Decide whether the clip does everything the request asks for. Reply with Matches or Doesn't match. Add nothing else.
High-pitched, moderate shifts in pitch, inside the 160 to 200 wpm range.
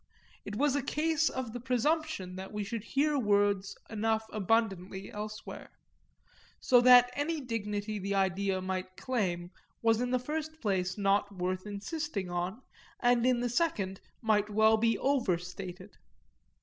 Doesn't match